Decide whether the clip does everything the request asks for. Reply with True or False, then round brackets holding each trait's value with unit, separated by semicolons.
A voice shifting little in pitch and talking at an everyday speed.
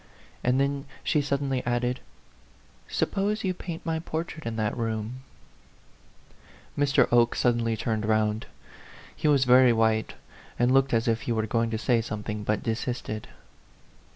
False (3.7 semitones; 150 wpm)